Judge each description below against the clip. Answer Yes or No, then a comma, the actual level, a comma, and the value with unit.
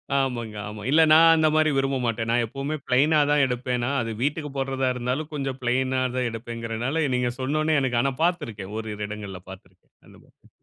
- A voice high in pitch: No, low, 130 Hz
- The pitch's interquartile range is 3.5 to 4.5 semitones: Yes, average, 4.0 semitones